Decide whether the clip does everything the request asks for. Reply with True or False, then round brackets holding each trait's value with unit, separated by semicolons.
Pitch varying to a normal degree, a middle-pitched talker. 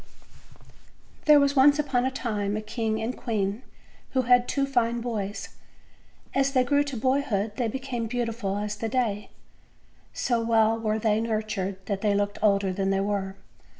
False (3.6 semitones; 225 Hz)